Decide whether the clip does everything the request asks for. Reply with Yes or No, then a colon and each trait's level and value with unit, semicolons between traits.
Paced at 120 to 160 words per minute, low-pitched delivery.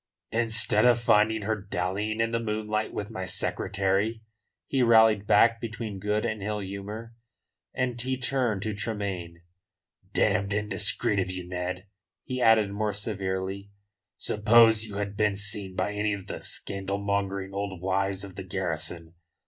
Yes: average, 150 wpm; low, 105 Hz